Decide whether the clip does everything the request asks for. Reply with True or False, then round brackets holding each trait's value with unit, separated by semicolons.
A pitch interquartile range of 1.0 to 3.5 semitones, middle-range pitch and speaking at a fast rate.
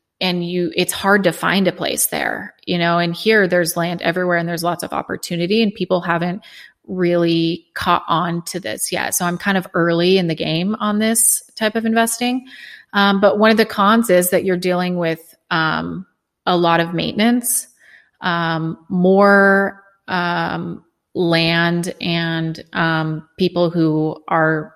False (2.9 semitones; 180 Hz; 165 wpm)